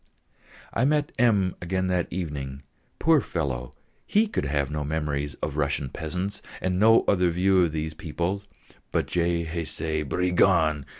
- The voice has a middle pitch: No, very low, 85 Hz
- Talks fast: No, average, 155 wpm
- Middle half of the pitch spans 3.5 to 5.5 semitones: Yes, average, 3.8 semitones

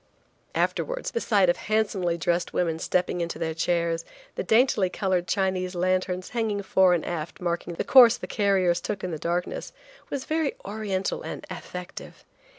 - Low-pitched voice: No, medium, 185 Hz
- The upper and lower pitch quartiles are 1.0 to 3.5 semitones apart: Yes, average, 3.0 semitones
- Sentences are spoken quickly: No, average, 160 wpm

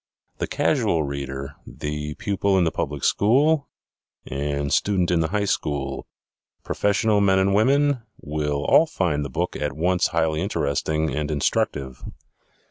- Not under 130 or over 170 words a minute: Yes, average, 140 wpm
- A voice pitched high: No, very low, 80 Hz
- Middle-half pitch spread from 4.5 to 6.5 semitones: Yes, wide, 5.5 semitones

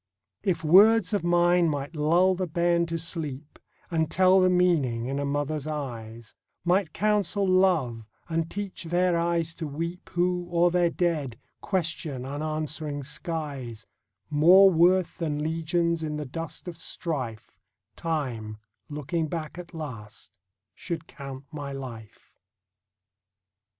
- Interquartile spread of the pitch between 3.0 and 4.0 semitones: Yes, average, 3.4 semitones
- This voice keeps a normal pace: No, slow, 130 wpm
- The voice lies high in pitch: No, medium, 160 Hz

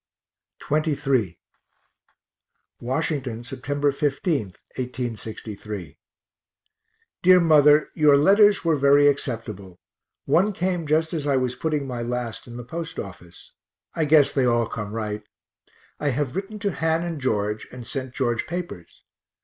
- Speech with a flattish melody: No, average, 5.0 semitones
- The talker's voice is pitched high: No, low, 135 Hz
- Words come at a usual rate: No, slow, 130 wpm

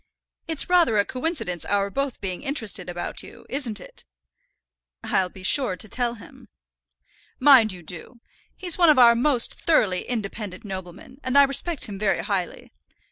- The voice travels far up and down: Yes, wide, 6.2 semitones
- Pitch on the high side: Yes, high, 225 Hz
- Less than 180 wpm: Yes, average, 160 wpm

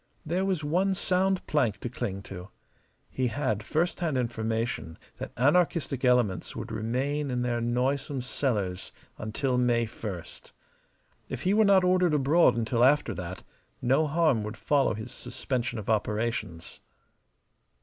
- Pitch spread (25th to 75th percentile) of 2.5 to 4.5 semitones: No, average, 5.0 semitones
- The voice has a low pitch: Yes, low, 125 Hz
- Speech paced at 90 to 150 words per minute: Yes, average, 140 wpm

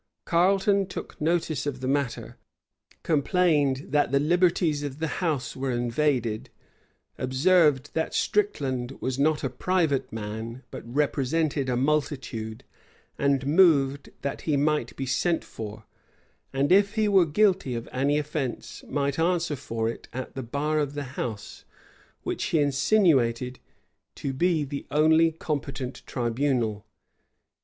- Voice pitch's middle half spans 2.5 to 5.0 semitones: Yes, average, 3.8 semitones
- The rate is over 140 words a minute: No, slow, 135 wpm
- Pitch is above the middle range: No, medium, 145 Hz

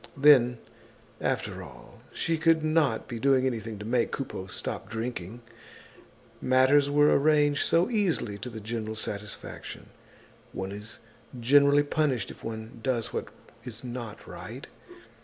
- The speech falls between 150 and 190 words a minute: No, slow, 135 wpm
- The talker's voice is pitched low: Yes, low, 125 Hz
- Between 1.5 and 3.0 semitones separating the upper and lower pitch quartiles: No, average, 4.5 semitones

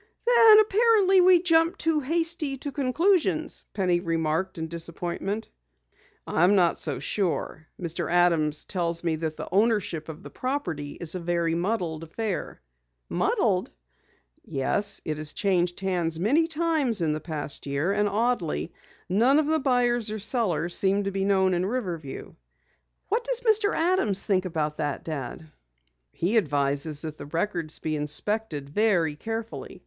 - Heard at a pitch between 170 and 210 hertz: Yes, high, 190 Hz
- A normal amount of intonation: No, wide, 7.5 semitones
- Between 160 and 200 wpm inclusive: No, average, 150 wpm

